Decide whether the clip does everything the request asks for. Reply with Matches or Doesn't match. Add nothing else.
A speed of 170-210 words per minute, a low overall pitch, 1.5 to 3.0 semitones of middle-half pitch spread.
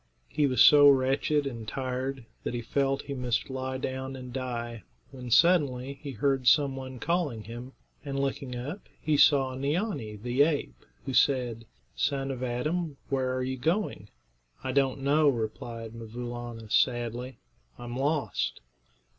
Doesn't match